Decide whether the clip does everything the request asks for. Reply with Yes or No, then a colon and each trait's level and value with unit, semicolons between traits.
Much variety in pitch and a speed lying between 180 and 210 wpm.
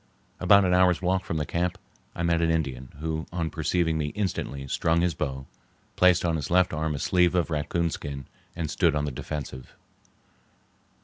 No: average, 3.1 semitones; average, 185 wpm